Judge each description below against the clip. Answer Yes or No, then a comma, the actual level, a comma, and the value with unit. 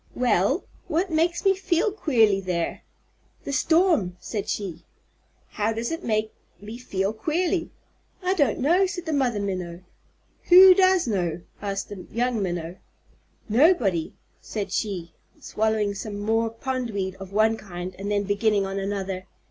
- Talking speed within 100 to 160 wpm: Yes, average, 145 wpm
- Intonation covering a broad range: Yes, wide, 7.6 semitones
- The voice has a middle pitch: No, high, 215 Hz